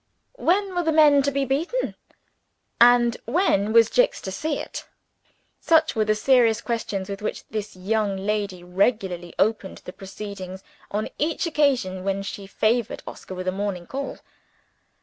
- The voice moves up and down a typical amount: No, wide, 6.2 semitones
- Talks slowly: No, average, 155 wpm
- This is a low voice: No, high, 215 Hz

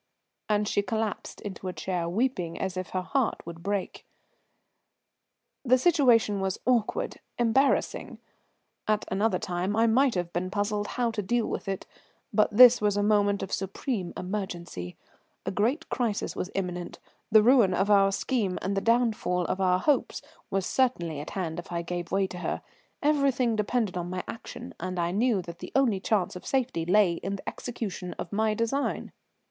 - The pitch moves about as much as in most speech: Yes, average, 4.1 semitones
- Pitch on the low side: No, high, 205 Hz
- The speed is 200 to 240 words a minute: No, average, 175 wpm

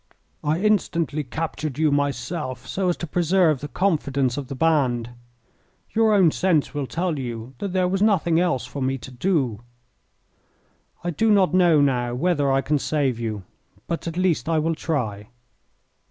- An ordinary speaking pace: Yes, average, 170 wpm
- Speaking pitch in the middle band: Yes, medium, 155 Hz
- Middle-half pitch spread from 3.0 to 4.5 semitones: No, average, 5.0 semitones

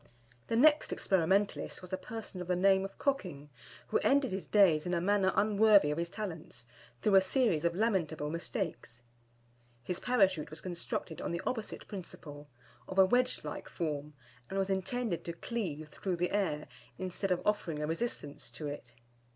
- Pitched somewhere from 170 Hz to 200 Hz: Yes, medium, 185 Hz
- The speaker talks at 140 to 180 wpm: Yes, average, 170 wpm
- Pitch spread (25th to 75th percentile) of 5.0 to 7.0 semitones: No, average, 4.4 semitones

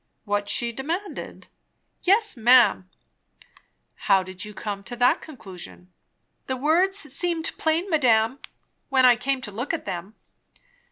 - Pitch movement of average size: No, wide, 7.4 semitones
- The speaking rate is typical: No, slow, 130 wpm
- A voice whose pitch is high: Yes, very high, 250 Hz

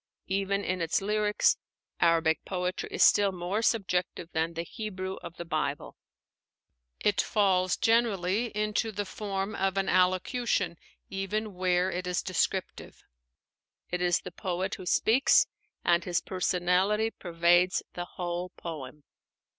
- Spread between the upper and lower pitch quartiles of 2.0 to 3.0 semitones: Yes, narrow, 2.4 semitones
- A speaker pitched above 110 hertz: Yes, medium, 185 Hz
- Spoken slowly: Yes, slow, 130 wpm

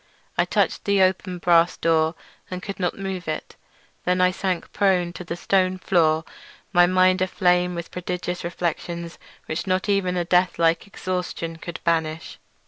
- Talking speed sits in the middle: Yes, average, 160 wpm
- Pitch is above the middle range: No, medium, 180 Hz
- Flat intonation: Yes, narrow, 1.6 semitones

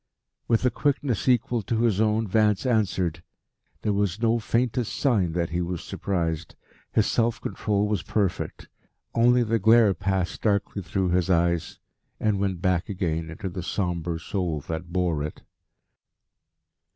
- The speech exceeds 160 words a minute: No, average, 150 wpm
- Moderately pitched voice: No, low, 100 Hz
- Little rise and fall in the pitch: No, average, 4.3 semitones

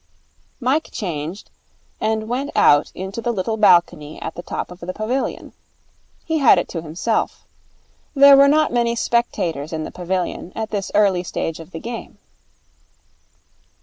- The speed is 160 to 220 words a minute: No, average, 150 wpm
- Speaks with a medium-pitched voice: No, high, 200 Hz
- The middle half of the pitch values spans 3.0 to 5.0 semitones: No, wide, 5.5 semitones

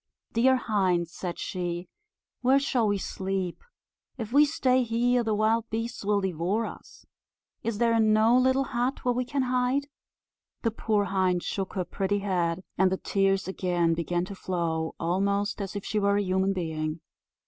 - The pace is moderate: Yes, average, 170 wpm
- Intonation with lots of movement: No, average, 4.2 semitones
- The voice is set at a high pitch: Yes, high, 200 Hz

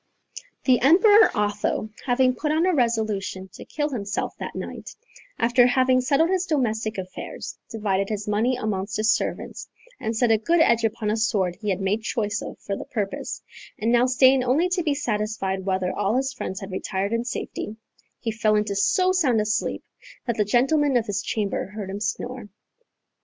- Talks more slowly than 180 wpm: No, average, 185 wpm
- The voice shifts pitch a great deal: No, average, 3.8 semitones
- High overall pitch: Yes, high, 225 Hz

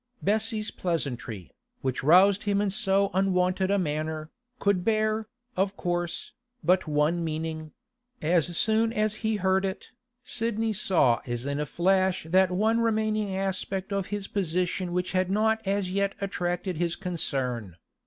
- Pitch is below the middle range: No, high, 190 Hz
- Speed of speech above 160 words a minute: No, average, 145 wpm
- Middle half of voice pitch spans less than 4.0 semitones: Yes, average, 3.3 semitones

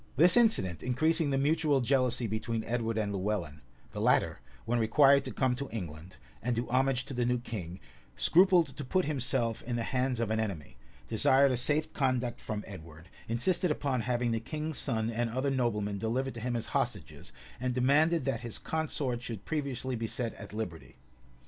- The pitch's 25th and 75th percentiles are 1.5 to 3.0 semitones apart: No, average, 3.7 semitones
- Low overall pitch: Yes, low, 125 Hz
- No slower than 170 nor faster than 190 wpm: Yes, average, 185 wpm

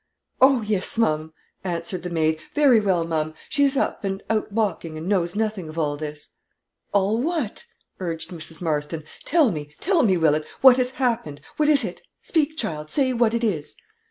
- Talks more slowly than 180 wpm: No, average, 185 wpm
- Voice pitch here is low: No, high, 195 Hz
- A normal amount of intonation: No, wide, 7.5 semitones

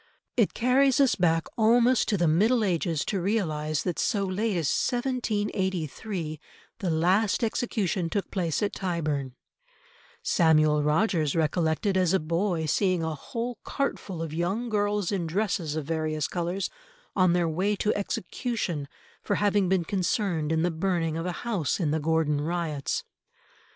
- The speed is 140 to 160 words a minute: Yes, average, 150 wpm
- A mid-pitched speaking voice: Yes, medium, 180 Hz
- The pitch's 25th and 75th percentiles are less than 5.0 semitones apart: Yes, average, 4.4 semitones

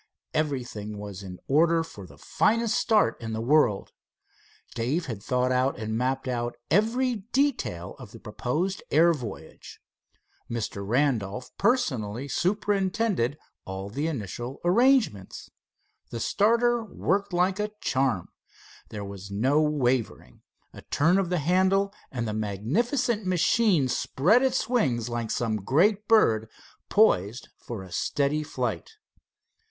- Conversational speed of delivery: No, slow, 130 wpm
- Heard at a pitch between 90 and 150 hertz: Yes, medium, 140 Hz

